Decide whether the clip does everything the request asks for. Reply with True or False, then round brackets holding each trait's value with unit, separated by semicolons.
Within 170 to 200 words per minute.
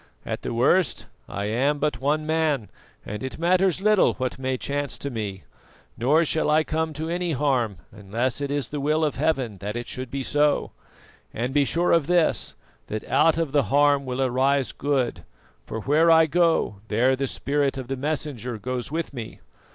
True (190 wpm)